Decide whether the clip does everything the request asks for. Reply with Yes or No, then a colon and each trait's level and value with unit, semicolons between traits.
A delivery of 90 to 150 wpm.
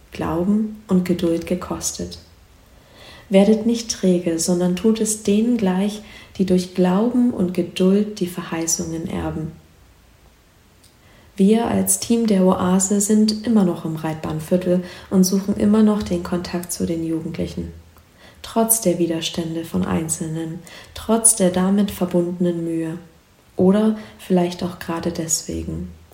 Yes: slow, 125 wpm